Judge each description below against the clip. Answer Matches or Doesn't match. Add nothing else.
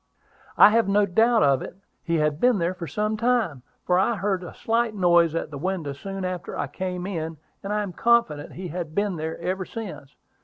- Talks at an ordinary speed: Doesn't match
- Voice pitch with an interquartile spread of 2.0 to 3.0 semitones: Doesn't match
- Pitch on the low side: Doesn't match